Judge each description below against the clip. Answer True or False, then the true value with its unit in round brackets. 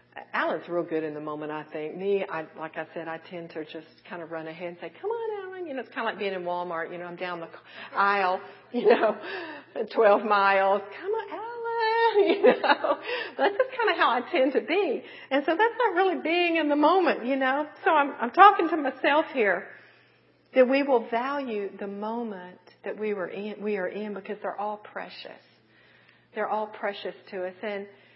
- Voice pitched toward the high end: True (210 Hz)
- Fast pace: True (215 wpm)